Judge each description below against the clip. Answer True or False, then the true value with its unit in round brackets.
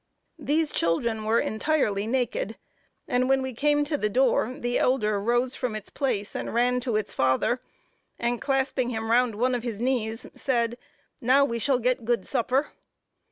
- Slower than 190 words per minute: True (170 wpm)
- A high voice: True (245 Hz)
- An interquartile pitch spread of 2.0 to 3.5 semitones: True (2.9 semitones)